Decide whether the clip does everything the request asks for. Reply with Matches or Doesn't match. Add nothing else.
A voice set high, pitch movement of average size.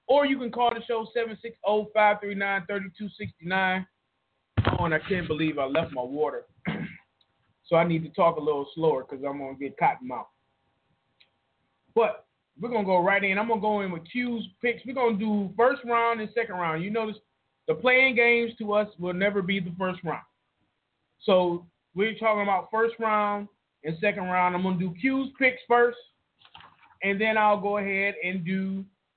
Matches